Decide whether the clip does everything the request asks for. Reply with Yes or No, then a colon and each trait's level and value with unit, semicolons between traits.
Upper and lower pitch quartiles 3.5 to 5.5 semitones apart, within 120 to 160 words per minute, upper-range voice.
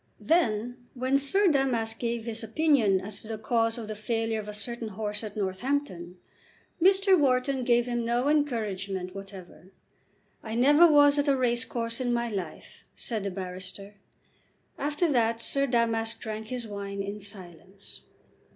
Yes: average, 3.9 semitones; average, 155 wpm; high, 230 Hz